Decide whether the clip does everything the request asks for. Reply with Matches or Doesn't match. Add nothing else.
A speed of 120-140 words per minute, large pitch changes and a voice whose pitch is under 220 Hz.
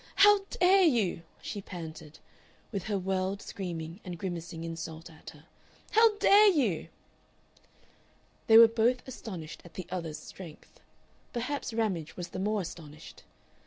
Matches